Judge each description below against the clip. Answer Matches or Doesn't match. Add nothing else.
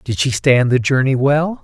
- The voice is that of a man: Matches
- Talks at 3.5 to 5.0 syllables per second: Matches